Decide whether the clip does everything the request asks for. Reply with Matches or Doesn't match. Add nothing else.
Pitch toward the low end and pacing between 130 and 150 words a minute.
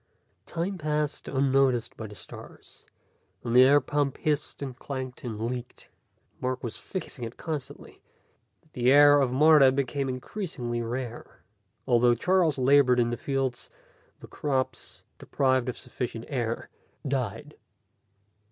Matches